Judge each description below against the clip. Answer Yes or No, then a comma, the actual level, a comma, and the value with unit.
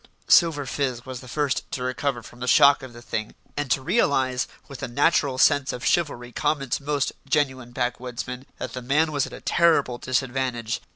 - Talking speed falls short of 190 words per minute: No, average, 195 wpm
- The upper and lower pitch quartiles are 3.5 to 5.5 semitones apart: No, narrow, 2.6 semitones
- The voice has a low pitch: Yes, low, 130 Hz